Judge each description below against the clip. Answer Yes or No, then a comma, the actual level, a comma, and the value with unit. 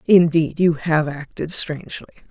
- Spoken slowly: Yes, slow, 130 wpm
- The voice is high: No, medium, 155 Hz